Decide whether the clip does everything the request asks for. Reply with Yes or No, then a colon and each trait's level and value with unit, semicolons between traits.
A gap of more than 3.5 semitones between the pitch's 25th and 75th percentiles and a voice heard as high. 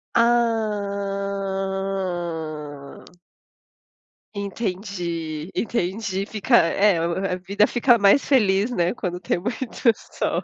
No: average, 3.2 semitones; high, 195 Hz